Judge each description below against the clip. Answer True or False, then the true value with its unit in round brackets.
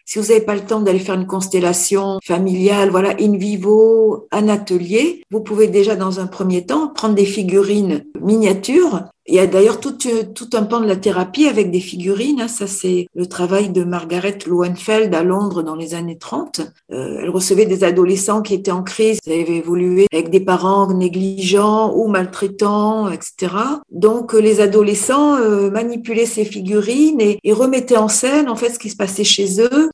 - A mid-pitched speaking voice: False (205 Hz)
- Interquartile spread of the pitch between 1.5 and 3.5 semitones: True (2.7 semitones)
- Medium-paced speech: True (185 wpm)